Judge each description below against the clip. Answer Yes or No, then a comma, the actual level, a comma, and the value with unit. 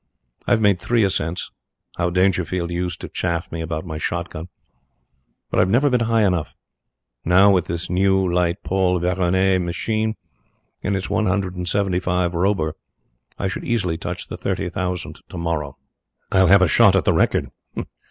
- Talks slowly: No, average, 170 wpm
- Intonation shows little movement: Yes, narrow, 2.2 semitones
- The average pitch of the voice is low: Yes, very low, 90 Hz